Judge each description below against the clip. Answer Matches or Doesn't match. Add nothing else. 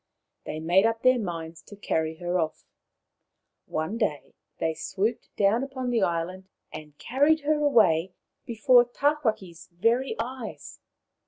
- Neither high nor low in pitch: Doesn't match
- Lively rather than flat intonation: Matches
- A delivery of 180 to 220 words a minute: Doesn't match